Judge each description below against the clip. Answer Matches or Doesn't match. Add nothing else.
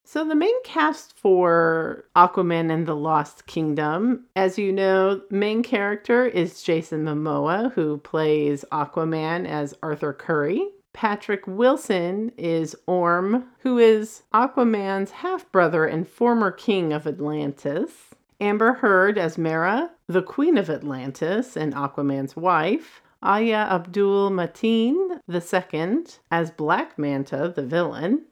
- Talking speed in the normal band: Doesn't match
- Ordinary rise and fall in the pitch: Doesn't match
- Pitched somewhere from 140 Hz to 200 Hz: Matches